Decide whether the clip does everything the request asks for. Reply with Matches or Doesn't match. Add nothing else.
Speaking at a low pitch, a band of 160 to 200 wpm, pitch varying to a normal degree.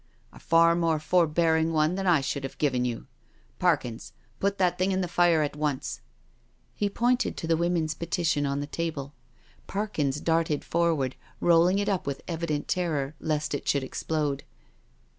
Doesn't match